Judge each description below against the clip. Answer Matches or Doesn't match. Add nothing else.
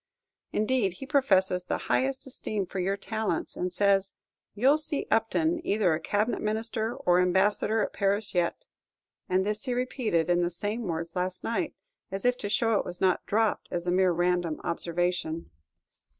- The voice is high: Matches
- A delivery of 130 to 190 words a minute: Matches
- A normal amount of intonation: Matches